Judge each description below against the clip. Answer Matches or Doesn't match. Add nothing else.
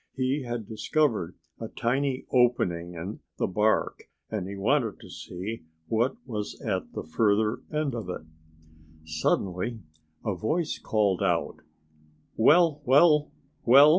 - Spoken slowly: Matches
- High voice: Doesn't match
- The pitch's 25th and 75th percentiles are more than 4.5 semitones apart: Matches